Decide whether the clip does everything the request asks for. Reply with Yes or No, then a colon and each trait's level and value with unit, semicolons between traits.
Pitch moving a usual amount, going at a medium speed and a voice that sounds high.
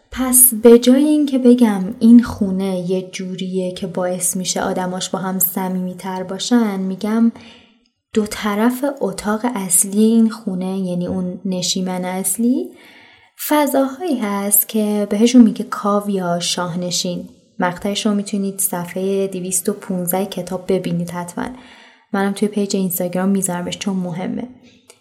Yes: average, 4.0 semitones; average, 125 wpm; high, 200 Hz